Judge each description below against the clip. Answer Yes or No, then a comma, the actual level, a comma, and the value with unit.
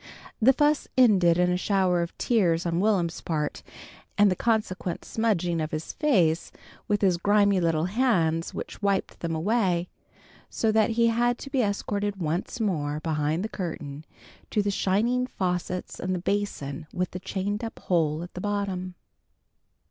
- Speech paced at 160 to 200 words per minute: Yes, average, 165 wpm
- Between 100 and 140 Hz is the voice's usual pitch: No, medium, 185 Hz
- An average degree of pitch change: Yes, average, 3.9 semitones